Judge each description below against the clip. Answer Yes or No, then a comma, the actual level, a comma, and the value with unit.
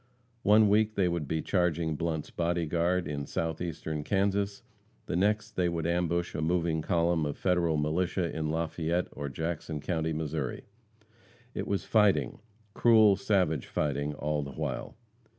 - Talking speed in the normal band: Yes, average, 150 wpm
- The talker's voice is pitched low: Yes, very low, 85 Hz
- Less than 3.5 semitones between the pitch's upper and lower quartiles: Yes, average, 2.9 semitones